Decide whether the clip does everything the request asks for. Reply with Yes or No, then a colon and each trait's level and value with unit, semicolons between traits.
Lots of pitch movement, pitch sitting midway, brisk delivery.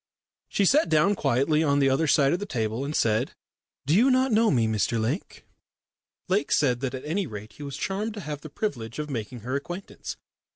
Yes: wide, 7.3 semitones; medium, 145 Hz; fast, 210 wpm